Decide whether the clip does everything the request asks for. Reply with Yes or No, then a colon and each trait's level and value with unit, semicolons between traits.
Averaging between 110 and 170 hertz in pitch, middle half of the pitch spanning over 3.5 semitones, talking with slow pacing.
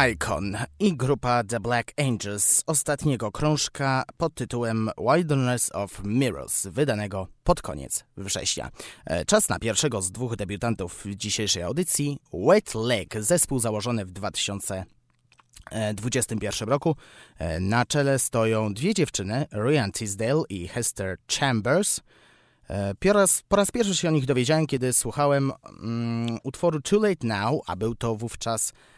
No: low, 115 Hz; wide, 5.6 semitones; average, 130 wpm